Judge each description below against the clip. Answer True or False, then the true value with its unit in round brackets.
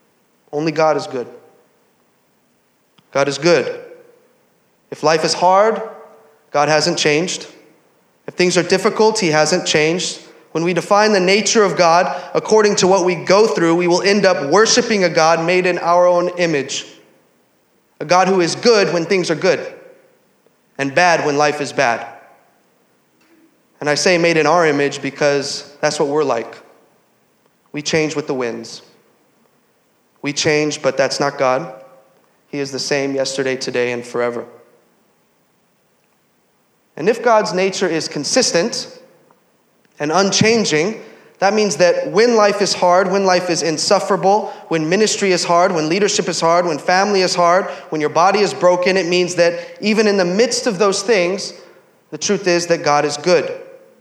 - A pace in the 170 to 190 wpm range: False (160 wpm)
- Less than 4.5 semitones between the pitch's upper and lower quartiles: False (4.9 semitones)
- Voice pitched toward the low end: False (175 Hz)